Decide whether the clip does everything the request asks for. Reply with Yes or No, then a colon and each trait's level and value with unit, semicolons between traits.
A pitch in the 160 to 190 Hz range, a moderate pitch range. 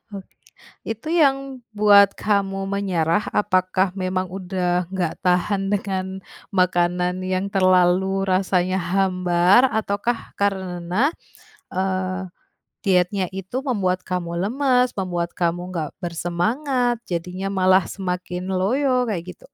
No: medium, 185 Hz; narrow, 2.0 semitones